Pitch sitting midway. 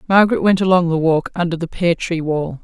Yes: medium, 170 Hz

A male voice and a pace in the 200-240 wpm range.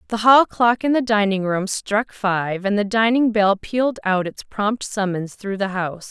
No: female; fast, 205 wpm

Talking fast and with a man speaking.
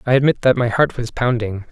Yes: fast, 245 wpm; male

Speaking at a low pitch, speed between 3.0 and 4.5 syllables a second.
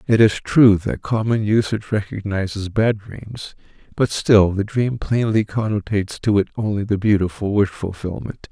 No: low, 105 Hz; 4.8 syllables/s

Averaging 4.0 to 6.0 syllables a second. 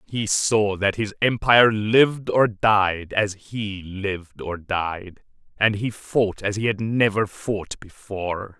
No: 3.6 syllables/s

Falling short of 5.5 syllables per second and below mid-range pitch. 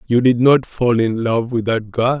Yes: 4.4 syllables/s; low, 120 Hz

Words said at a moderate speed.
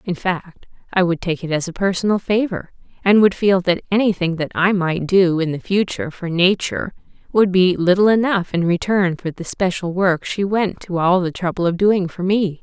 No: fast, 210 wpm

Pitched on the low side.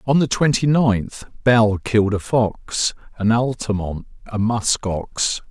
Yes: low, 110 Hz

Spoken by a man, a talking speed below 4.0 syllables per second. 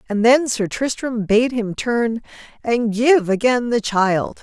No: female; 3.7 syllables/s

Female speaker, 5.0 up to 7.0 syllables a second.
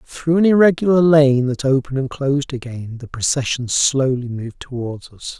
No: male; 5.2 syllables/s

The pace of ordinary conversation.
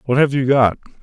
No: fast, 235 wpm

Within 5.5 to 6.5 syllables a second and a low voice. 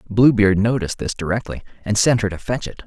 Yes: 6.2 syllables/s; low, 110 Hz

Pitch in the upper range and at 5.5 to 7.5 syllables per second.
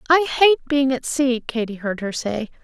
No: very high, 260 Hz; 4.8 syllables/s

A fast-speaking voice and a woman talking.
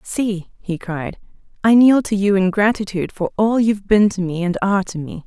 Yes: fast, 215 wpm; female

